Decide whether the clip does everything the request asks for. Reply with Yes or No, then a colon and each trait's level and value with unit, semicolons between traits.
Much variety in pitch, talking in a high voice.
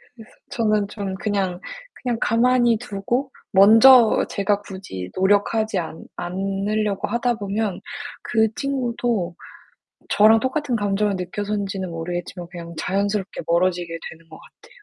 No: average, 3.3 semitones; high, 205 Hz